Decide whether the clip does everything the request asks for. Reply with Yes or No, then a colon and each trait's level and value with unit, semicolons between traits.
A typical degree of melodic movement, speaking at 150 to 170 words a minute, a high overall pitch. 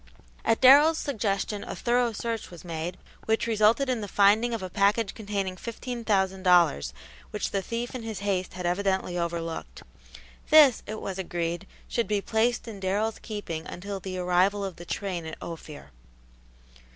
Yes: average, 3.9 semitones; average, 165 wpm; high, 200 Hz